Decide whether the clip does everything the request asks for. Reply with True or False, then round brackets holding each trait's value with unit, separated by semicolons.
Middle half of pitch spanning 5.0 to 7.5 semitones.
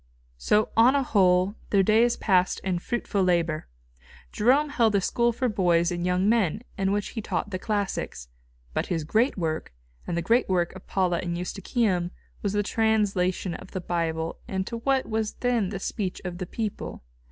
False (3.7 semitones)